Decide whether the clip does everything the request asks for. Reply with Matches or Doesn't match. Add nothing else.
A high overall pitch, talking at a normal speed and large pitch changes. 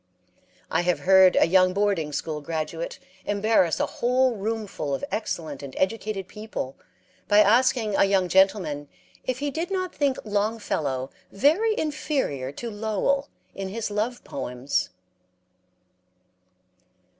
Doesn't match